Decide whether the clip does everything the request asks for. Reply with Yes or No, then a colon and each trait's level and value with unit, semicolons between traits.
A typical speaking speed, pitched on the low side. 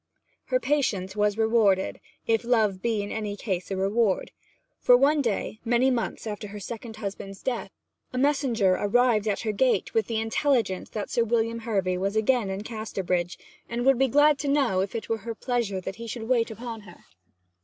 No: average, 190 wpm; high, 225 Hz